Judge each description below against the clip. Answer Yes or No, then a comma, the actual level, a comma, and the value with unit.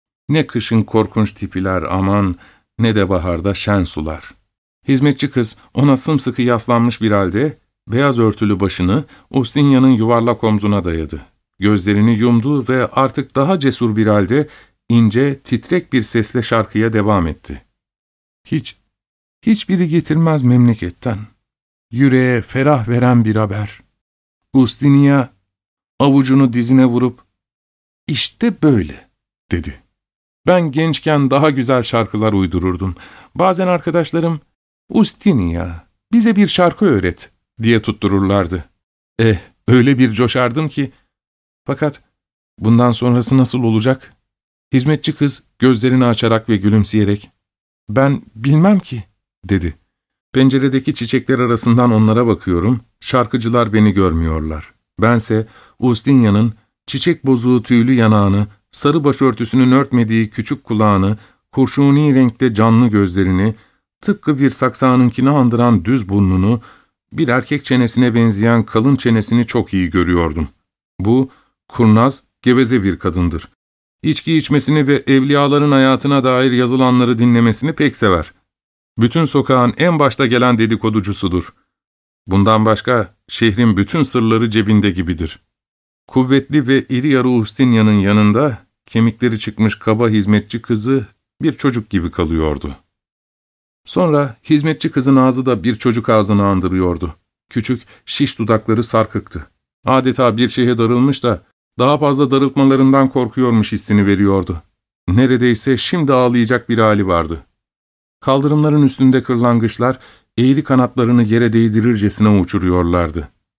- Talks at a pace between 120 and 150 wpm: No, average, 110 wpm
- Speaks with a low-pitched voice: Yes, low, 120 Hz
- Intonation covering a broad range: No, average, 4.2 semitones